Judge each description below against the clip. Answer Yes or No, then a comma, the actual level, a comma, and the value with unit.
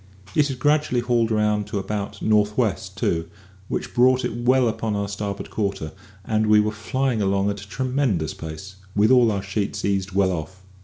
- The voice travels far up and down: No, average, 3.5 semitones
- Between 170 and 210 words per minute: Yes, average, 190 wpm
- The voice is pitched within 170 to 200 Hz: No, low, 105 Hz